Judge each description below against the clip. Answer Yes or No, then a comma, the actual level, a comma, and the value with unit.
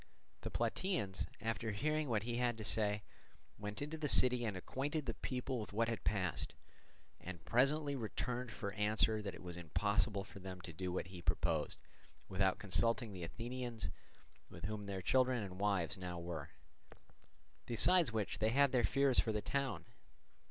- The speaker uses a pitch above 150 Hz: No, low, 110 Hz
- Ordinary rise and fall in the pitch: Yes, average, 4.6 semitones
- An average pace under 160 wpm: No, average, 170 wpm